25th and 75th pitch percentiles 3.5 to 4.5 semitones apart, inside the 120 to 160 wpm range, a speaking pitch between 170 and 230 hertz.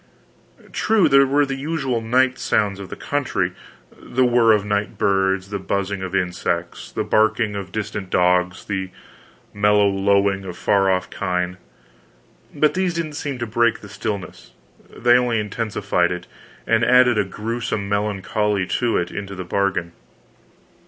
No: average, 3.9 semitones; average, 150 wpm; low, 105 Hz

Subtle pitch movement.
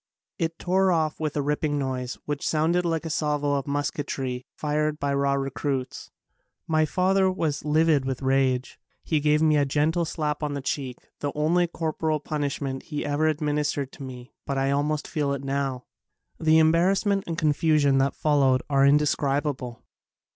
Yes: narrow, 2.3 semitones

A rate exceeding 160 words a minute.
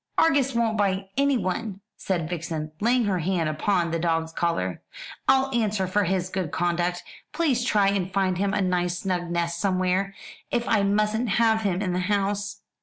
Yes: average, 175 wpm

